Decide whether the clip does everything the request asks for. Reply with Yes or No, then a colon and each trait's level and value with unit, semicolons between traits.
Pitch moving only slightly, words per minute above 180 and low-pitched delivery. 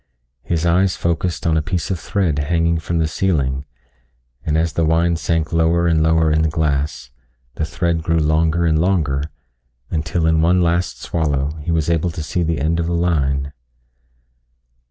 No: narrow, 1.7 semitones; average, 175 wpm; very low, 80 Hz